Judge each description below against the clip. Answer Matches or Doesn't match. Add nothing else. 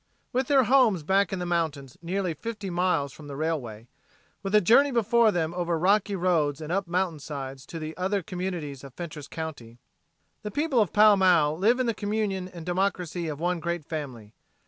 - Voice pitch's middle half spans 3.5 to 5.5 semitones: Matches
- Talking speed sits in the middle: Matches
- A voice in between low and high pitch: Matches